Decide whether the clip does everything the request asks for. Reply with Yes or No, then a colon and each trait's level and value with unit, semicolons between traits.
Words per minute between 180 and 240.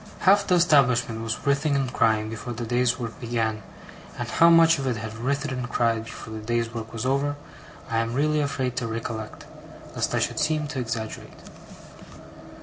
Yes: average, 185 wpm